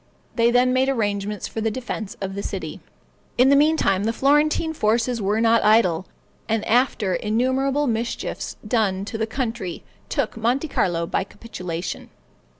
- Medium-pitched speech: No, high, 225 Hz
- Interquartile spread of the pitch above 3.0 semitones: Yes, average, 4.0 semitones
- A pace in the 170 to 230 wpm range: No, average, 150 wpm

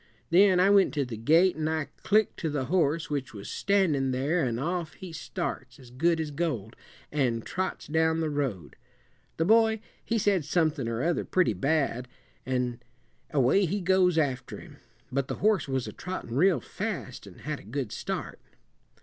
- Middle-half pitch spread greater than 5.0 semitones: Yes, wide, 5.6 semitones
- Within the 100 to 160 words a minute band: No, average, 180 wpm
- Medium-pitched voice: Yes, medium, 155 Hz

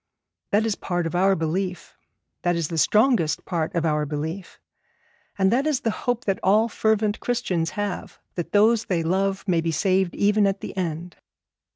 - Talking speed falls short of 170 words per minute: No, average, 180 wpm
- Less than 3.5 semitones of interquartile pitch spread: No, average, 3.9 semitones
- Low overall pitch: No, high, 190 Hz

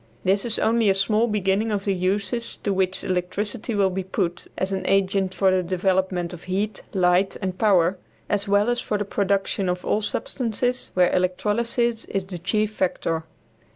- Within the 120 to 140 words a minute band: No, average, 180 wpm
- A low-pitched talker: No, high, 195 Hz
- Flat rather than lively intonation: Yes, narrow, 2.2 semitones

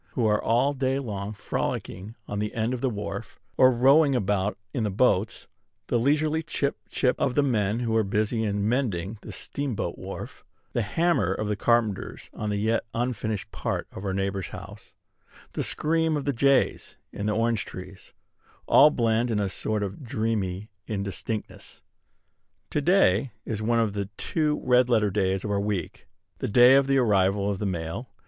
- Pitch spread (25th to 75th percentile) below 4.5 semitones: Yes, average, 4.0 semitones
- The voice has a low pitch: Yes, low, 110 Hz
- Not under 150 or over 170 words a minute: No, average, 180 wpm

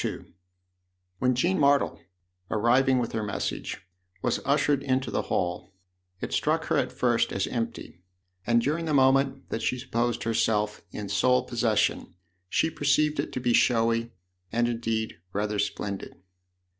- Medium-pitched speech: No, low, 120 Hz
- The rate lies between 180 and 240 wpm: No, average, 145 wpm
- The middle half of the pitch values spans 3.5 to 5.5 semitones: No, average, 3.1 semitones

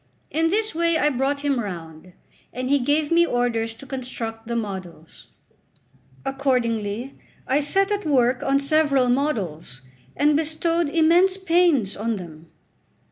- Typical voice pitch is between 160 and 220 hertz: No, very high, 270 Hz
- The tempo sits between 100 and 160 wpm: Yes, slow, 135 wpm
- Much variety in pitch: Yes, wide, 5.7 semitones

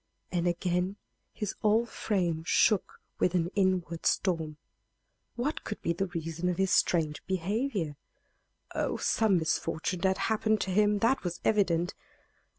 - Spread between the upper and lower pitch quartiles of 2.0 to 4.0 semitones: Yes, average, 3.7 semitones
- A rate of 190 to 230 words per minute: No, average, 140 wpm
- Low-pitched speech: No, medium, 185 Hz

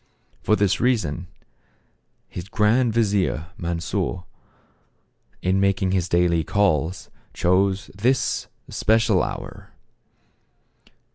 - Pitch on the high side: No, very low, 95 Hz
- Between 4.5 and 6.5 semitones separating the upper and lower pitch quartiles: No, average, 3.3 semitones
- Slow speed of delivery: Yes, slow, 85 wpm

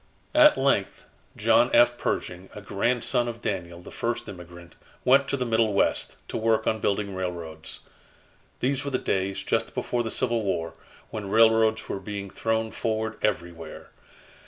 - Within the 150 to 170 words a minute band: Yes, average, 155 wpm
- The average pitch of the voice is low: Yes, low, 110 Hz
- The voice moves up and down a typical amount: Yes, average, 3.5 semitones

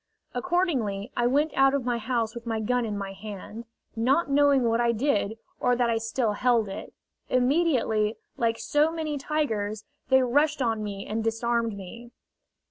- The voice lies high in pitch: Yes, high, 235 Hz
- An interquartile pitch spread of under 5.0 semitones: Yes, average, 3.7 semitones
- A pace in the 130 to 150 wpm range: No, average, 170 wpm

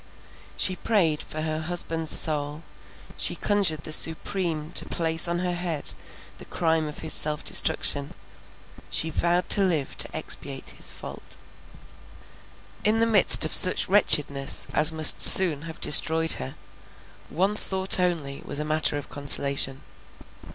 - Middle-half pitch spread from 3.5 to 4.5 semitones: No, average, 3.0 semitones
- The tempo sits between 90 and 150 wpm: Yes, slow, 135 wpm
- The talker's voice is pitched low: No, medium, 160 Hz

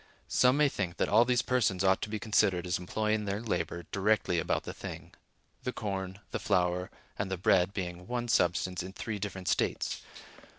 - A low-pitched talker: Yes, low, 100 Hz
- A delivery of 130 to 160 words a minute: No, average, 185 wpm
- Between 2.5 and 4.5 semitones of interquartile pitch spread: Yes, average, 3.1 semitones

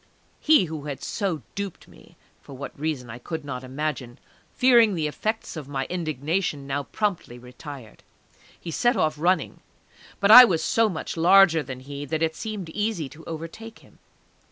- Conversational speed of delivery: Yes, average, 170 wpm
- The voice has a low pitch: No, medium, 160 Hz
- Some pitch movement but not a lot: No, wide, 5.7 semitones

